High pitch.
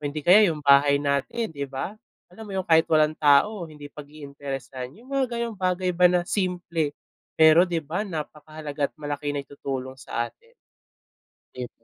No: medium, 155 Hz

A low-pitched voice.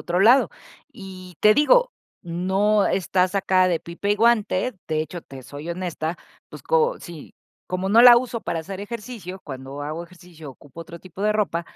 No: medium, 185 Hz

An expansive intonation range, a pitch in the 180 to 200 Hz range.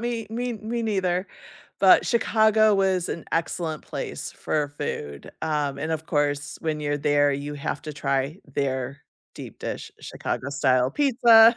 No: wide, 7.2 semitones; medium, 155 Hz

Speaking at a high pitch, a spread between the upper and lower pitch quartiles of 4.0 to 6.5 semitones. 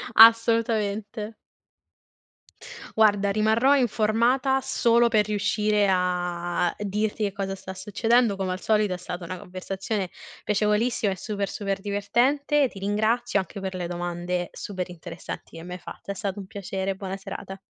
No: high, 200 Hz; average, 2.7 semitones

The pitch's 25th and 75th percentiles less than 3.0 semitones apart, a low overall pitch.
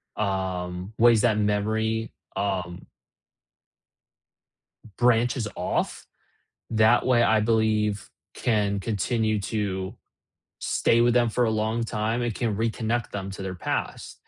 Yes: narrow, 2.4 semitones; low, 110 Hz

